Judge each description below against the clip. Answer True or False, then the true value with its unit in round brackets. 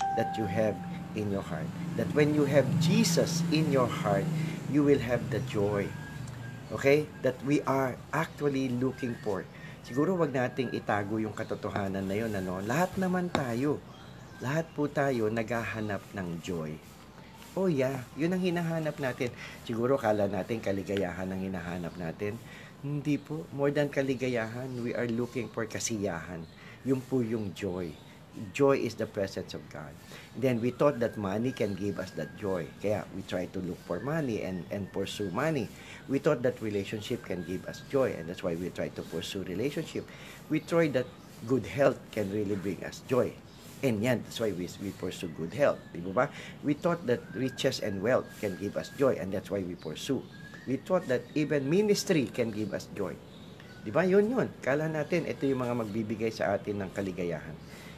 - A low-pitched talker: True (125 Hz)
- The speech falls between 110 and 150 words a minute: False (180 wpm)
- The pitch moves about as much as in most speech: False (6.4 semitones)